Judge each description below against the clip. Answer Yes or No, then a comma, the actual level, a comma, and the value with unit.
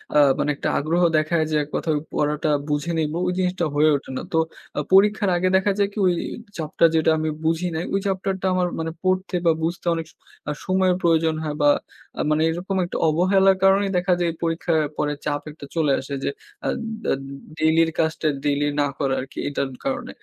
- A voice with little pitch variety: No, average, 3.3 semitones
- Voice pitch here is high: No, medium, 165 Hz